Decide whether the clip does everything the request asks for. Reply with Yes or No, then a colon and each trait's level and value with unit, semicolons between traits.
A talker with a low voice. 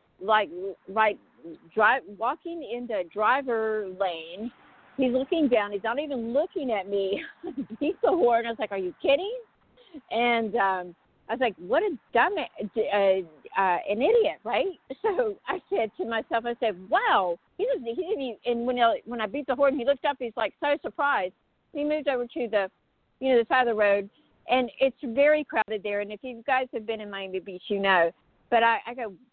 No: high, 235 Hz